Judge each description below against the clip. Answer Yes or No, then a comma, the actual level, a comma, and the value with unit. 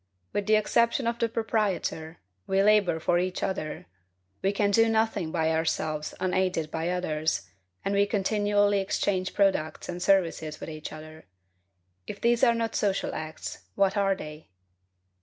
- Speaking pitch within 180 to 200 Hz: Yes, high, 190 Hz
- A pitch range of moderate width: Yes, average, 4.4 semitones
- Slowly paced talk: No, average, 155 wpm